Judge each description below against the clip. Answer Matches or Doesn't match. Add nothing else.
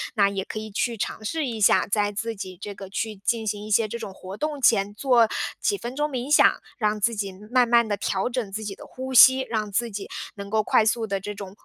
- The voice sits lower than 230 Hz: Matches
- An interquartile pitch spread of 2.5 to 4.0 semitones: Matches